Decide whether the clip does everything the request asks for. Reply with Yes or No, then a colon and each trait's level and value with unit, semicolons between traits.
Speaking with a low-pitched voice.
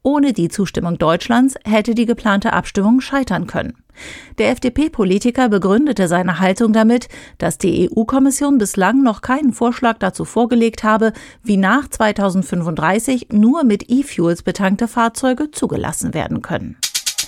No: high, 225 Hz